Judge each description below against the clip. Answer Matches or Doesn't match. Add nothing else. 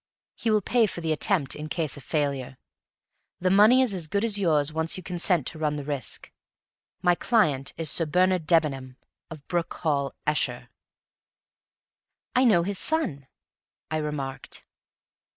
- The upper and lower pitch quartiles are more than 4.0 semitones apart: Matches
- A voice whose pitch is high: Doesn't match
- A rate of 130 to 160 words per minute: Matches